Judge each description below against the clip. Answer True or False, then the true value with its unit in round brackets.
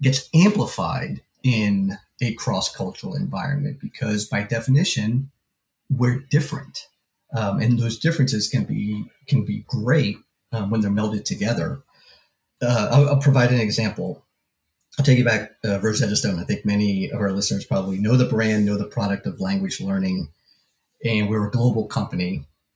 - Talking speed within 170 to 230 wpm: False (155 wpm)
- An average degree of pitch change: True (4.7 semitones)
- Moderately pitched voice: False (115 Hz)